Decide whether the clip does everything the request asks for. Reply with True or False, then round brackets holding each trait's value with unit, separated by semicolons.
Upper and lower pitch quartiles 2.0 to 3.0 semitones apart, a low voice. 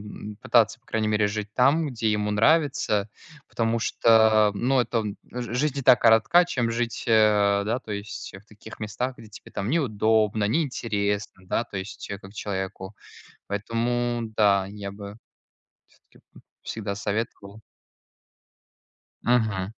True (2.5 semitones; 110 Hz)